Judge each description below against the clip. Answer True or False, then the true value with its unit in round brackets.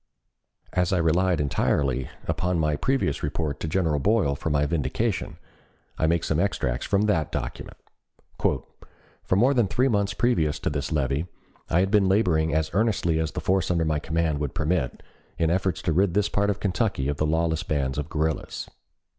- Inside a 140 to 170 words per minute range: False (180 wpm)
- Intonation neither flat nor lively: True (4.1 semitones)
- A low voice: True (80 Hz)